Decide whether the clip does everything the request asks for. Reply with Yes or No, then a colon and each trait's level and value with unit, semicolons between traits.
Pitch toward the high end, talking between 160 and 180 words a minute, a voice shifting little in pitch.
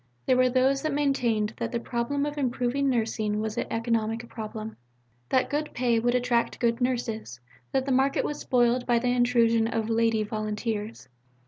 Yes: high, 235 Hz; average, 175 wpm; narrow, 2.3 semitones